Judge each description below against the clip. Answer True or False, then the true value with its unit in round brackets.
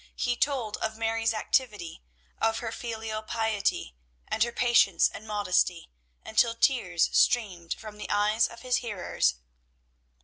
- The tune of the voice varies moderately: False (2.2 semitones)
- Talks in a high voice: True (220 Hz)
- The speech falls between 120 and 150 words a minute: True (135 wpm)